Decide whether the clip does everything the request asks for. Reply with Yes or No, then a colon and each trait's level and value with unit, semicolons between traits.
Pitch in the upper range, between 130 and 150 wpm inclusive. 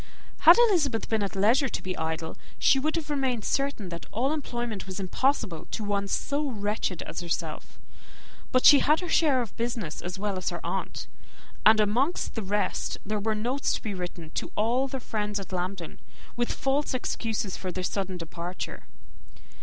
No: high, 215 Hz; average, 180 wpm